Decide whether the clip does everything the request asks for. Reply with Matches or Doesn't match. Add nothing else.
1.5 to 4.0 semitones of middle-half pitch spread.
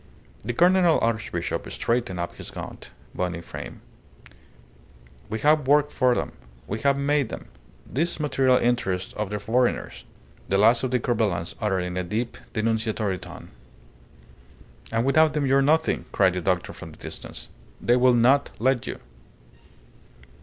Doesn't match